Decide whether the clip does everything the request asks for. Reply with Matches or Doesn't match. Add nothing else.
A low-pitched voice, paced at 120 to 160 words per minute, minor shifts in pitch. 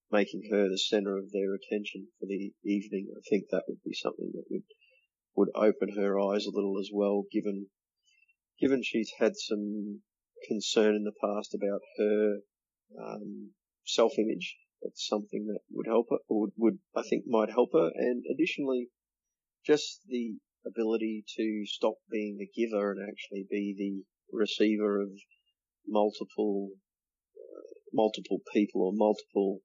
Matches